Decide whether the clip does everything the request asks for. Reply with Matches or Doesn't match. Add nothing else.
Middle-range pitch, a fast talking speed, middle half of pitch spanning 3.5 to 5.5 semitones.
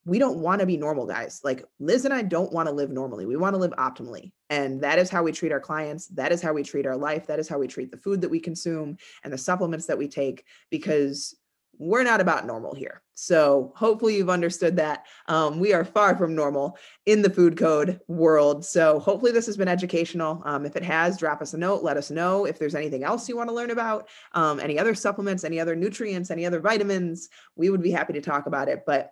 Matches